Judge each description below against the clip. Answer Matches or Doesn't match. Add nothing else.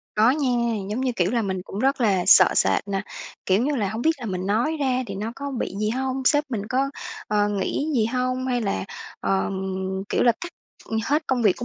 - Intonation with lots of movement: Doesn't match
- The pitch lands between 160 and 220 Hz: Doesn't match